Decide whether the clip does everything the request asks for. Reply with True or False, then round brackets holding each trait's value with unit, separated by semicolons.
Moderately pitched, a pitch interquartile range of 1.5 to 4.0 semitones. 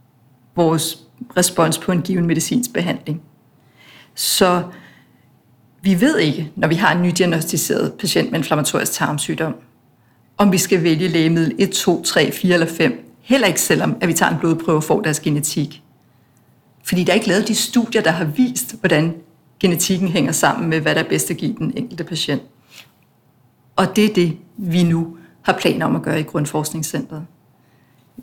True (165 Hz; 3.5 semitones)